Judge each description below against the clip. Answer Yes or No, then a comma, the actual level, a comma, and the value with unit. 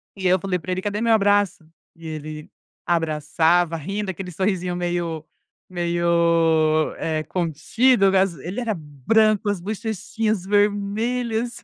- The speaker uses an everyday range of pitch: Yes, average, 3.8 semitones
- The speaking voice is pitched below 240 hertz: Yes, medium, 185 Hz